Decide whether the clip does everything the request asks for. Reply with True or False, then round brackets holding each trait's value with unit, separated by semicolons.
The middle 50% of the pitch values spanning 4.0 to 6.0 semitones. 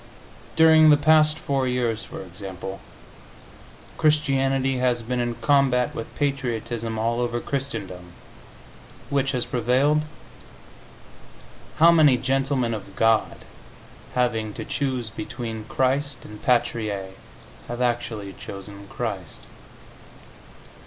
False (3.6 semitones)